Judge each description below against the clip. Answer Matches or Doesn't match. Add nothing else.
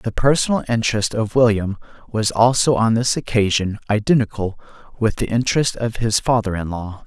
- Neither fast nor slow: Matches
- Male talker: Matches